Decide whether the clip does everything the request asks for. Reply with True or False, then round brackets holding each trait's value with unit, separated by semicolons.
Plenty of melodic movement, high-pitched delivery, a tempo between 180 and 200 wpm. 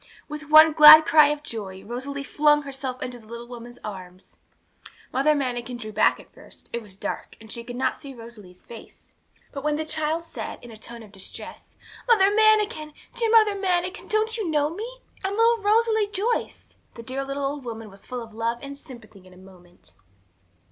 True (6.1 semitones; 275 Hz; 195 wpm)